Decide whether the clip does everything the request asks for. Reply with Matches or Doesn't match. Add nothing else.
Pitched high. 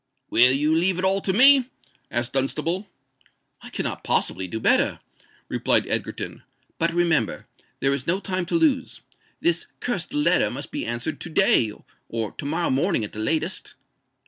Doesn't match